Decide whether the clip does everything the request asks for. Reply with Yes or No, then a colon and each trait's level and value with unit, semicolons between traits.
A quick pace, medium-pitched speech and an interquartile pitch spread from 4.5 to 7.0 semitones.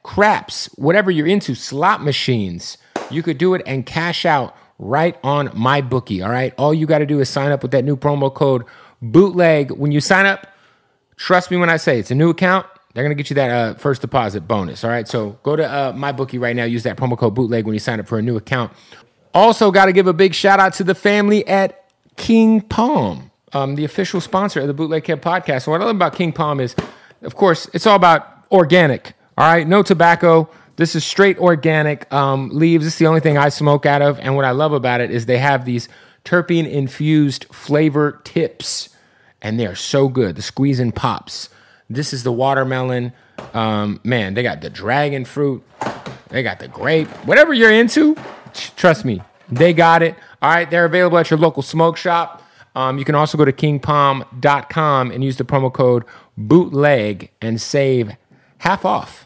Yes: fast, 210 wpm; medium, 145 Hz; average, 4.9 semitones